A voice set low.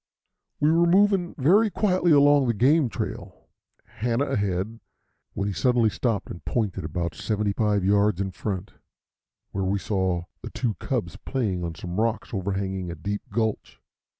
Yes: low, 105 Hz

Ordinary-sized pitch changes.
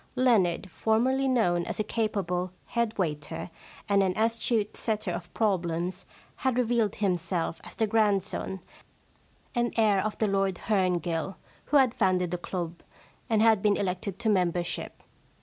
Yes: average, 3.8 semitones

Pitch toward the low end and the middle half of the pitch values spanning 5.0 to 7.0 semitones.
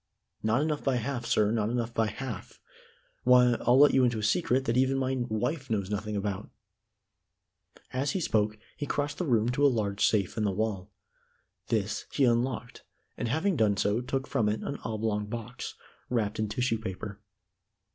No: low, 115 Hz; average, 3.6 semitones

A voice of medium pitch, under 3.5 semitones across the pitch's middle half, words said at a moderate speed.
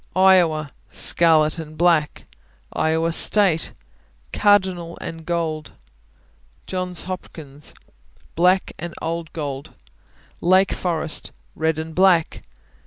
No: medium, 165 Hz; narrow, 2.5 semitones; slow, 95 wpm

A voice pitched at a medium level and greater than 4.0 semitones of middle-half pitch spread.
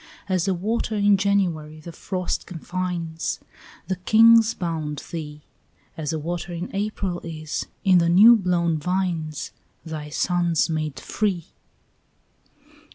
No: medium, 175 Hz; average, 3.3 semitones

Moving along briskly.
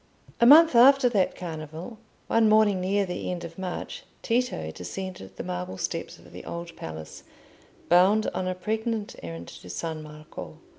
No: average, 160 wpm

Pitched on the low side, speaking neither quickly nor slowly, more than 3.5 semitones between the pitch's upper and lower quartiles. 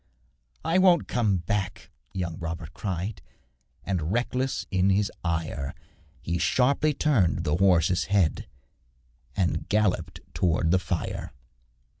No: very low, 95 Hz; slow, 115 wpm; average, 4.0 semitones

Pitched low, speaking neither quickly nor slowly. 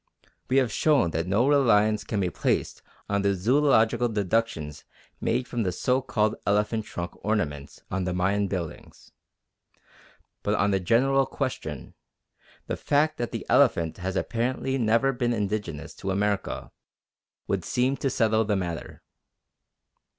Yes: low, 105 Hz; average, 145 wpm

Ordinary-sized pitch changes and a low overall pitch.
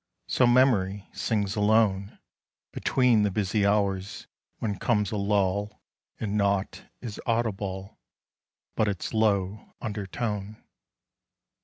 No: narrow, 1.8 semitones; low, 105 Hz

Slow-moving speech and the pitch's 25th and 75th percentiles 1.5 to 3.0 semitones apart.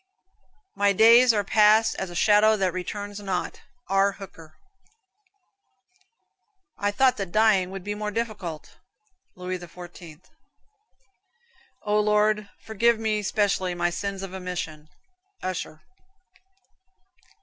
Yes: slow, 110 wpm; average, 2.7 semitones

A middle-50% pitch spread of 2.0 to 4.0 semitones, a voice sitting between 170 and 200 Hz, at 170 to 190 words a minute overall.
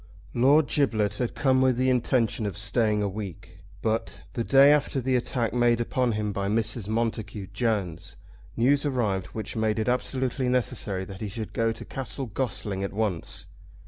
No: average, 3.6 semitones; low, 115 Hz; average, 175 wpm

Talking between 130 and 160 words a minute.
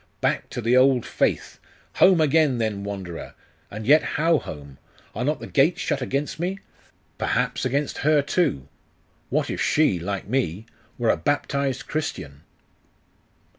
Yes: average, 145 wpm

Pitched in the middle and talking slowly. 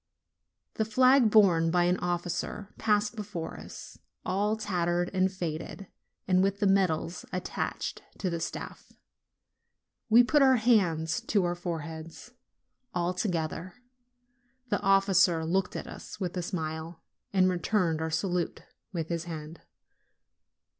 Yes: medium, 180 Hz; slow, 130 wpm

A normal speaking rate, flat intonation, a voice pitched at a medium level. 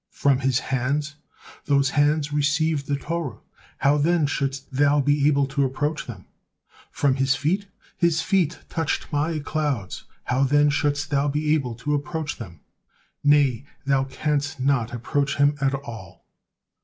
Yes: average, 150 wpm; narrow, 1.7 semitones; medium, 145 Hz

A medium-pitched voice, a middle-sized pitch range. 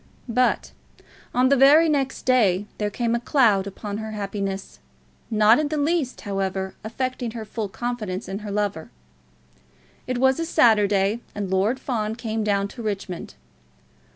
No: high, 220 Hz; average, 4.1 semitones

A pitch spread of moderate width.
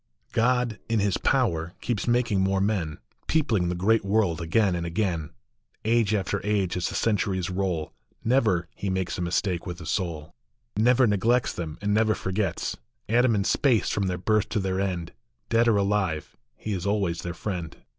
Yes: average, 3.8 semitones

